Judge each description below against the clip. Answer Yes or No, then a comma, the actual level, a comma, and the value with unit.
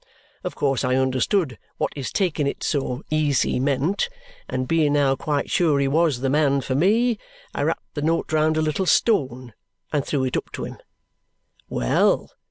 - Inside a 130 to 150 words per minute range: No, average, 180 wpm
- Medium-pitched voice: Yes, medium, 145 Hz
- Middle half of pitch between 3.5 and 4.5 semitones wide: No, average, 3.1 semitones